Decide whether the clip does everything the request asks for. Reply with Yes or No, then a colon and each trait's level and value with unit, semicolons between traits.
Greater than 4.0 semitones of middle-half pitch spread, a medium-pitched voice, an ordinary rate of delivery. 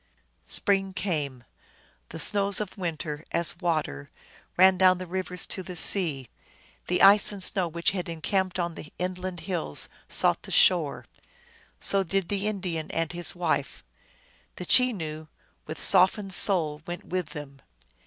No: average, 3.0 semitones; medium, 180 Hz; average, 145 wpm